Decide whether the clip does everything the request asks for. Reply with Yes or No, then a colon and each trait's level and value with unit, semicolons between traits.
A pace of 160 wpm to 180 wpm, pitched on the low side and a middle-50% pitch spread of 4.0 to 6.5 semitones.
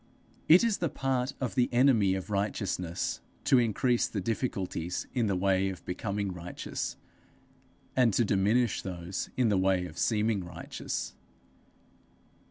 No: average, 140 wpm; low, 100 Hz; average, 4.7 semitones